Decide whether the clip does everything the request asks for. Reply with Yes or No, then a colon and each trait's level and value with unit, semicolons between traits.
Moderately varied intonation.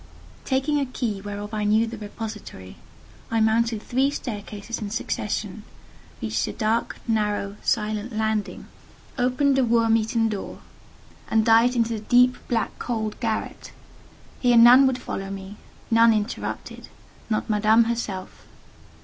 No: narrow, 2.0 semitones